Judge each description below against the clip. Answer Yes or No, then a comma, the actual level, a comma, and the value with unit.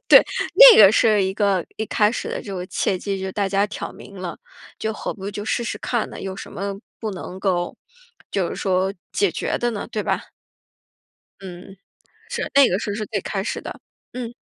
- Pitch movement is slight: Yes, narrow, 2.2 semitones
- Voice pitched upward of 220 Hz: No, high, 200 Hz